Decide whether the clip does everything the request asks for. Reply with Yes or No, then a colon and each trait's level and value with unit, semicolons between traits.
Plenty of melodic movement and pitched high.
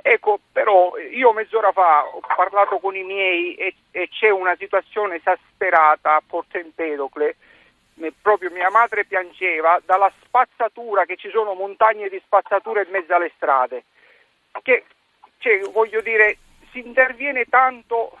No: average, 5.0 semitones; high, 200 Hz